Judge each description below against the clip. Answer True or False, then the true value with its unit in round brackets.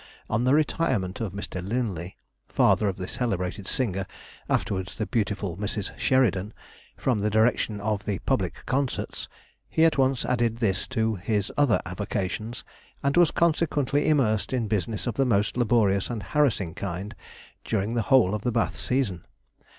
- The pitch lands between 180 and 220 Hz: False (110 Hz)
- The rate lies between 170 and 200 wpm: False (160 wpm)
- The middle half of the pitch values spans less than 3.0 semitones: False (4.3 semitones)